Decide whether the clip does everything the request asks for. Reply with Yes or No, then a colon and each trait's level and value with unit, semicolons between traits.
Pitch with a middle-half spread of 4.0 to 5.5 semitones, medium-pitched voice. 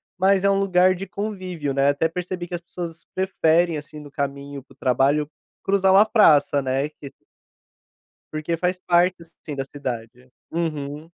Yes: average, 4.4 semitones; medium, 165 Hz